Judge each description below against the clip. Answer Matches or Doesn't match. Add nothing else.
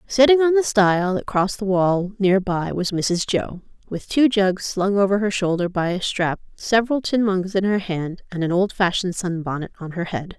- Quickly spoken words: Matches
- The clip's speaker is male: Doesn't match